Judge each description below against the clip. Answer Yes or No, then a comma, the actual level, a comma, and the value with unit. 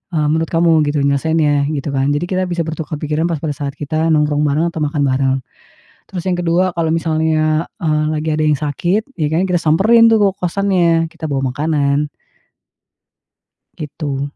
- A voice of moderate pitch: Yes, medium, 155 Hz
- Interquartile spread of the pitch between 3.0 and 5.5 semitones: No, narrow, 2.4 semitones